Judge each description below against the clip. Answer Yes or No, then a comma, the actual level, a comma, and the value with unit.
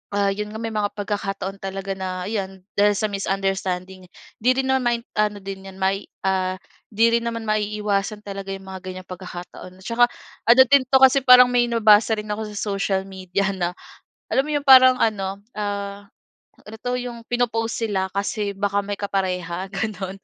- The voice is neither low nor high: No, high, 200 Hz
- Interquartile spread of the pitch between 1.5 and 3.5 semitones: Yes, average, 2.9 semitones